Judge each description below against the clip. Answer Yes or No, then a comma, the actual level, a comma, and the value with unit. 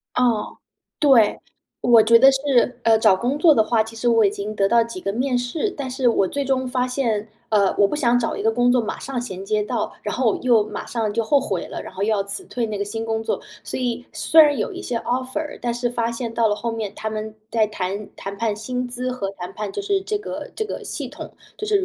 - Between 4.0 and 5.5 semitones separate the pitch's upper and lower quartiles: No, average, 3.0 semitones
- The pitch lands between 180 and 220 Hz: No, high, 235 Hz